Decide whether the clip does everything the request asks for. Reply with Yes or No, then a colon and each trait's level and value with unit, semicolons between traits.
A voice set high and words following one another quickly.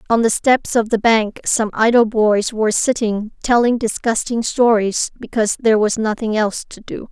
No: high, 225 Hz; average, 175 wpm